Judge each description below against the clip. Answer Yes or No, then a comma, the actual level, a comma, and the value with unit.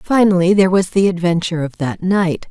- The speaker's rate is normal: Yes, average, 190 wpm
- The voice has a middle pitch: Yes, medium, 180 Hz